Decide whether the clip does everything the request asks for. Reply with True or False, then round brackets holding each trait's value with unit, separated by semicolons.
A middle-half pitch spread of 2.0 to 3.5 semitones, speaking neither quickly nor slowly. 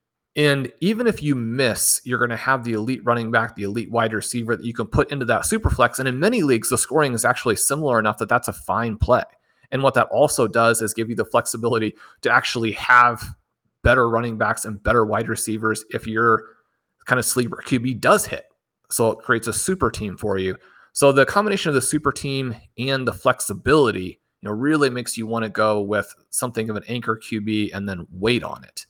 False (3.0 semitones; 220 wpm)